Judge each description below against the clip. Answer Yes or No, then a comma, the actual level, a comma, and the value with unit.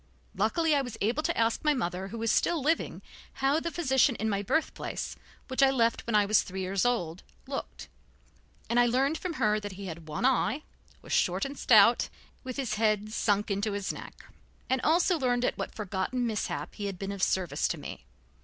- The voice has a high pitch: Yes, high, 230 Hz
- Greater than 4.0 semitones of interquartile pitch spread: Yes, average, 5.1 semitones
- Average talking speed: No, fast, 210 wpm